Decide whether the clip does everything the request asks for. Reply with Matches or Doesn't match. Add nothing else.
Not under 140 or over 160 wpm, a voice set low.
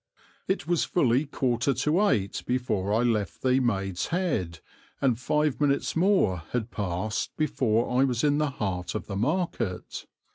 Matches